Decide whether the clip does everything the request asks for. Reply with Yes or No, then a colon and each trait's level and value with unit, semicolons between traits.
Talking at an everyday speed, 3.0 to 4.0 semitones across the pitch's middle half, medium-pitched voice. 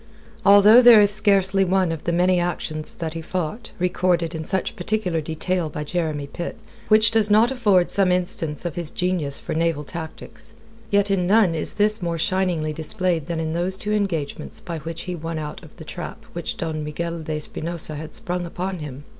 Yes: average, 195 wpm; average, 3.3 semitones; medium, 175 Hz